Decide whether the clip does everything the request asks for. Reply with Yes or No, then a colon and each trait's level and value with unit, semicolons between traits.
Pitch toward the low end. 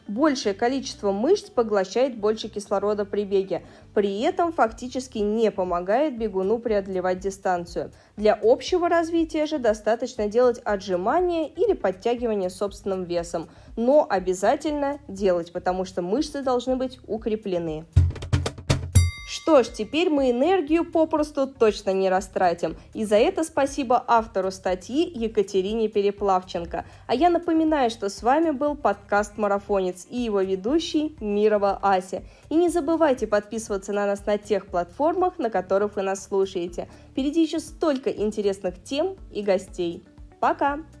No: high, 215 Hz